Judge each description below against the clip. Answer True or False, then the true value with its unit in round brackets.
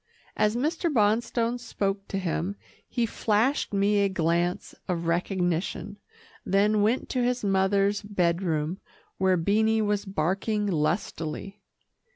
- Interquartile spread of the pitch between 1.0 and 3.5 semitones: True (3.1 semitones)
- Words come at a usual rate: False (125 wpm)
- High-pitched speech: True (200 Hz)